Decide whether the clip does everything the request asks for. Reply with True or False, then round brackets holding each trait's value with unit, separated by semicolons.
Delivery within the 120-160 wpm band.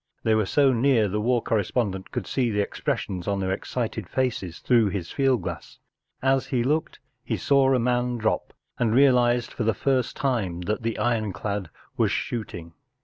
False (175 wpm)